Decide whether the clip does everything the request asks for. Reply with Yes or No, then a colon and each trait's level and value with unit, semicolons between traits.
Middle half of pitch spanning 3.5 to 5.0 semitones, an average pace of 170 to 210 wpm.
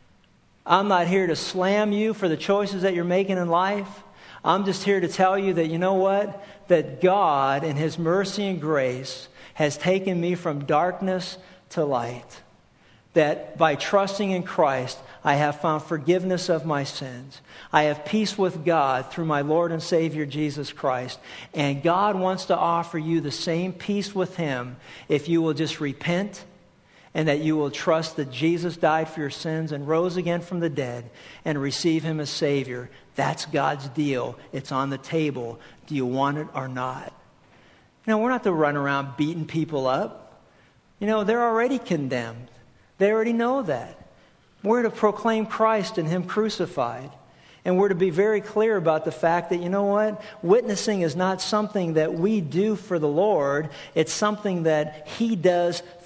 Yes: average, 4.6 semitones; average, 185 wpm